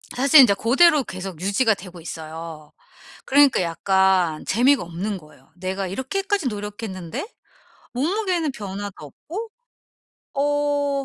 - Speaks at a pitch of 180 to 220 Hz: Yes, high, 205 Hz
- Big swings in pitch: Yes, wide, 7.5 semitones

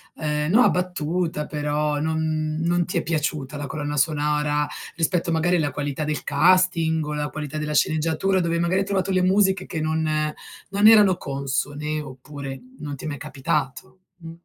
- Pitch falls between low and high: Yes, medium, 155 Hz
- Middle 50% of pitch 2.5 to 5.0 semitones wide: Yes, average, 2.9 semitones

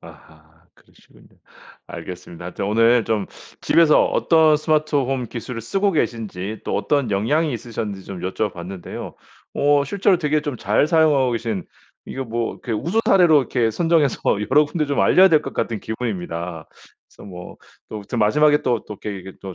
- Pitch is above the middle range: No, low, 120 Hz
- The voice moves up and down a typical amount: No, wide, 6.9 semitones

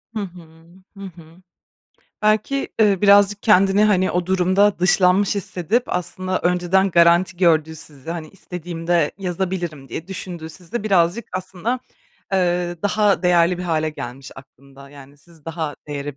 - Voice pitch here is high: No, medium, 180 Hz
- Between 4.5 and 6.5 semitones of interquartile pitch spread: No, average, 3.0 semitones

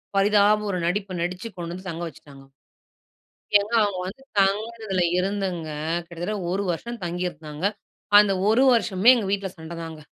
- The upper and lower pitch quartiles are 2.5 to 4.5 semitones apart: Yes, average, 3.3 semitones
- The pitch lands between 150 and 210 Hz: Yes, high, 190 Hz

